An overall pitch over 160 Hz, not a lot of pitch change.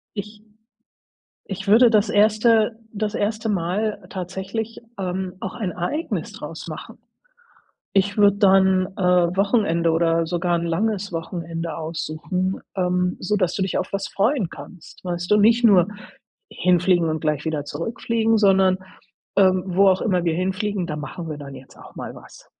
No: high, 190 Hz; average, 3.3 semitones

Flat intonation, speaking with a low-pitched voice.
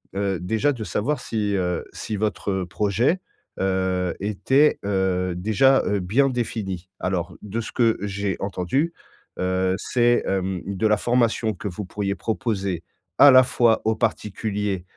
No: average, 3.4 semitones; low, 100 Hz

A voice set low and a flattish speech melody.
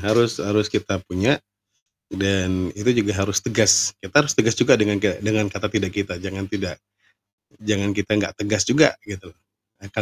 Yes: low, 100 Hz; narrow, 1.6 semitones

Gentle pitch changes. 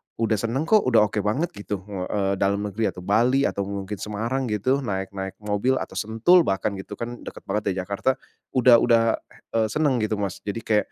No: average, 3.3 semitones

